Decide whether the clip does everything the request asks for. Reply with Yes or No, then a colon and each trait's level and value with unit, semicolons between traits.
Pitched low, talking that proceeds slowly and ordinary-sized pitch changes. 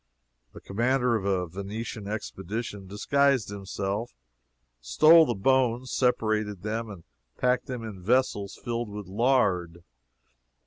Yes: low, 110 Hz; slow, 120 wpm; average, 4.1 semitones